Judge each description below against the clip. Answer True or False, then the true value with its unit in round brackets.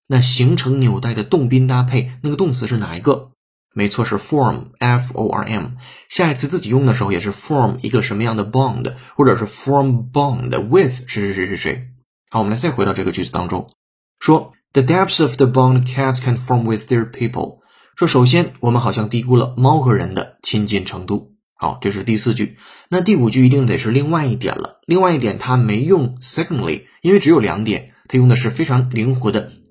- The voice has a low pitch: True (125 Hz)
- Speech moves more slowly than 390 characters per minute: False (400 characters per minute)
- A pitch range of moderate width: True (3.6 semitones)